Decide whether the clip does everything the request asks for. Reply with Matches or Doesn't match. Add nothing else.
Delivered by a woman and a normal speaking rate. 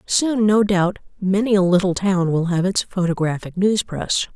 Matches